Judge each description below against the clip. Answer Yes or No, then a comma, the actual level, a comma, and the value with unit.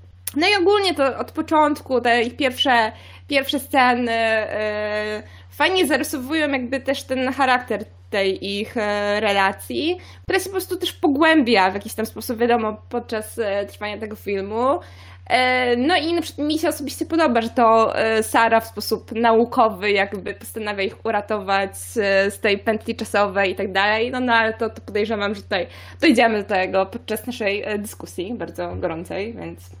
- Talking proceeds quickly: Yes, fast, 165 wpm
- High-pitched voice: Yes, high, 225 Hz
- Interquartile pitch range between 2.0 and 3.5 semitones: No, average, 4.6 semitones